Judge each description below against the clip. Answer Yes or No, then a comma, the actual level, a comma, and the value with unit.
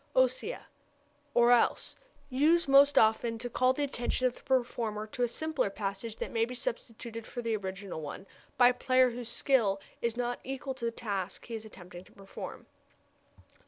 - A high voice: Yes, high, 240 Hz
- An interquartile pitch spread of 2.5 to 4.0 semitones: Yes, average, 2.9 semitones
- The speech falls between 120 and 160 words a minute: No, average, 180 wpm